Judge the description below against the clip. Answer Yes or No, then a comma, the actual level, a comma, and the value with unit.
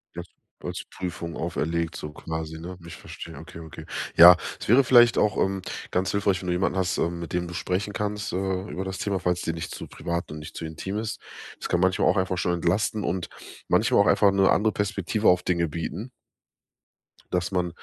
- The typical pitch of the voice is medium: No, very low, 90 Hz